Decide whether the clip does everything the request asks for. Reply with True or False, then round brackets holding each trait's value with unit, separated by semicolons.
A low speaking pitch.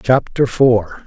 True (120 Hz)